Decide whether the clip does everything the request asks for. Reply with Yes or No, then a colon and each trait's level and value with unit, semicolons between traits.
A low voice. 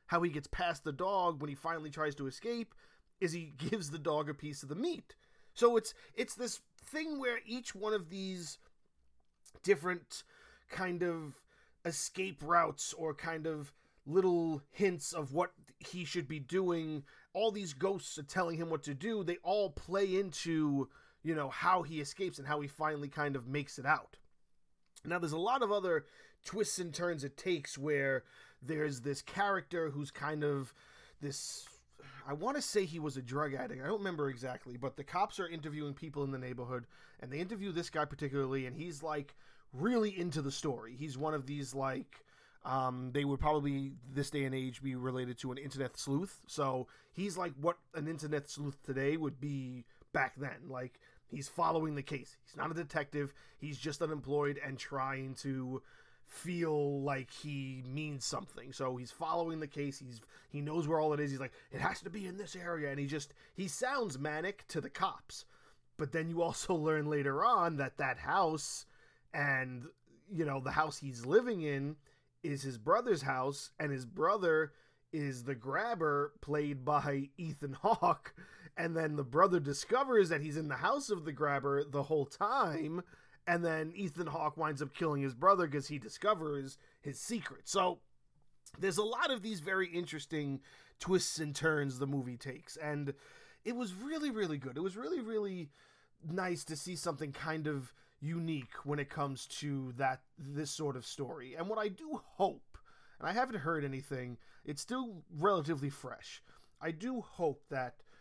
No: medium, 150 Hz